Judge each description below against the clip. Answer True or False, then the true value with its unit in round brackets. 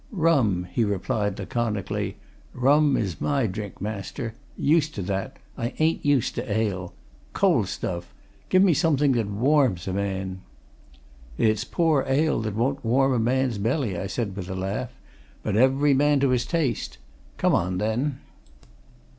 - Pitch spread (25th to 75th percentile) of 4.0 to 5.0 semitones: False (5.6 semitones)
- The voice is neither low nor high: False (115 Hz)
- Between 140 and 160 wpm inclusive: True (155 wpm)